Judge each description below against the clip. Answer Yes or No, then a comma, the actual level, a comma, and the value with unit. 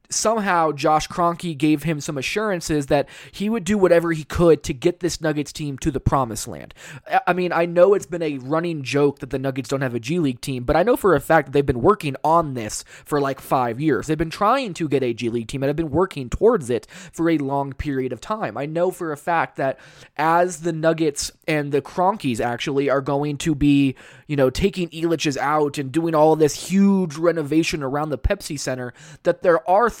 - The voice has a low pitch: No, medium, 155 Hz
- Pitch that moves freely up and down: No, average, 3.7 semitones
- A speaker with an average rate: No, fast, 225 wpm